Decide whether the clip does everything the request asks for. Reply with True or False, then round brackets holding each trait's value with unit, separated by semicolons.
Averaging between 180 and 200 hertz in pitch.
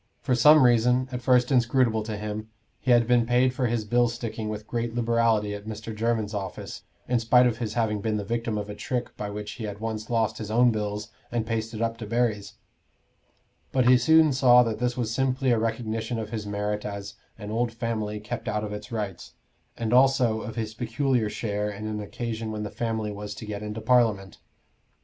False (115 Hz)